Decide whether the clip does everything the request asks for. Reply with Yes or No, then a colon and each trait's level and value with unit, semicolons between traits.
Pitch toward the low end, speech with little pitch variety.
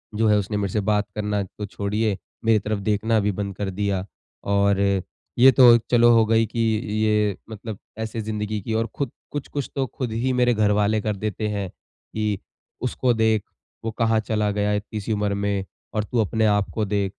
Yes: low, 105 Hz; narrow, 1.6 semitones